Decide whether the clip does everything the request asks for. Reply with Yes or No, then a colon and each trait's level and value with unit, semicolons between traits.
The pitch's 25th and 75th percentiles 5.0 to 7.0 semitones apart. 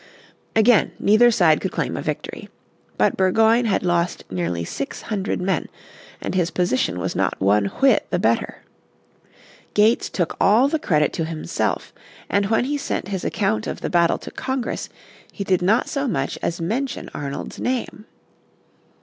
Yes: wide, 5.5 semitones